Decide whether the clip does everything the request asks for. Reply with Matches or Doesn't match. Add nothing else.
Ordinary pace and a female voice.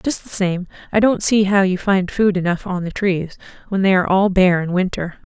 Doesn't match